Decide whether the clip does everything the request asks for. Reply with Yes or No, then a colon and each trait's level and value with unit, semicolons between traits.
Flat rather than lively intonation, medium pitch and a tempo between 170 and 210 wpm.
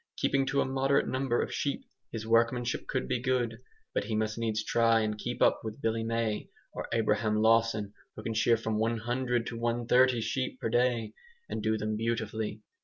No: narrow, 1.8 semitones; low, 115 Hz; average, 185 wpm